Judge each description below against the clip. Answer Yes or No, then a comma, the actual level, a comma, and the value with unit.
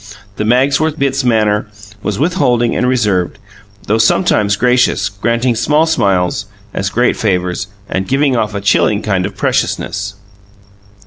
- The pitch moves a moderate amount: Yes, average, 4.1 semitones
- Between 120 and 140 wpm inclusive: Yes, slow, 135 wpm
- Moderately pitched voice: No, low, 110 Hz